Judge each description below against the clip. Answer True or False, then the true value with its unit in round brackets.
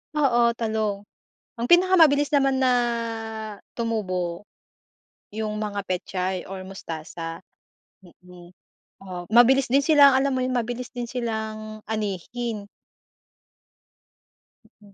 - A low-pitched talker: False (220 Hz)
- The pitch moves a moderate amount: True (4.9 semitones)